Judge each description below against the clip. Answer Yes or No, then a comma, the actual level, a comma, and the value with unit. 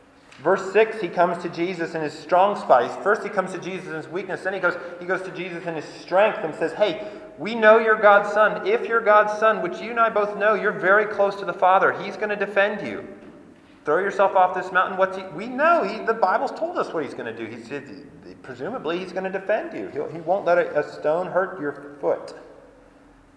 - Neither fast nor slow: No, fast, 240 wpm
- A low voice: No, high, 190 Hz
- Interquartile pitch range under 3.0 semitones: No, average, 3.4 semitones